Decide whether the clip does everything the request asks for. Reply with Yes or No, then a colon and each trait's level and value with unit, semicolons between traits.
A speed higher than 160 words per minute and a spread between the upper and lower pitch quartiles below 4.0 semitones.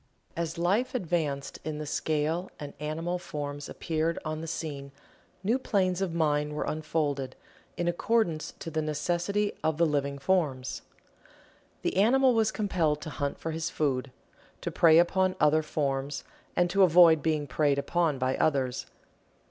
No: average, 155 wpm; average, 3.1 semitones